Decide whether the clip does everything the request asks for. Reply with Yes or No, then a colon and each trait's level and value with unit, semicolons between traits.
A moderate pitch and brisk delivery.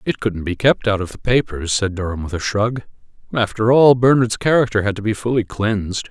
No: low, 110 Hz; fast, 215 wpm